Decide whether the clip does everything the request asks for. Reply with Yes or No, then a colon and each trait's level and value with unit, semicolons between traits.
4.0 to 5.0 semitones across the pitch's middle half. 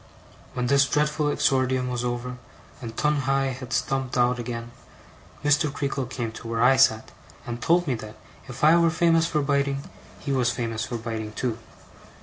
No: average, 2.8 semitones